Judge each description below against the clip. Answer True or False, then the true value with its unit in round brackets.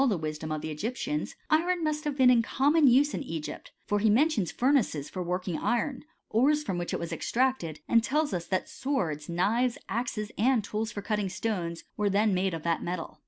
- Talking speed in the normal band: False (225 wpm)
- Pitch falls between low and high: False (215 Hz)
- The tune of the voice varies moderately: False (7.0 semitones)